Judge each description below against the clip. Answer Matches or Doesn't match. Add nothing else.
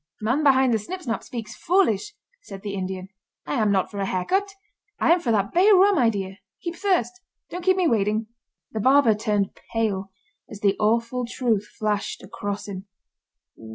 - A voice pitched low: Doesn't match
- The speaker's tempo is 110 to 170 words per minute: Doesn't match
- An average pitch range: Doesn't match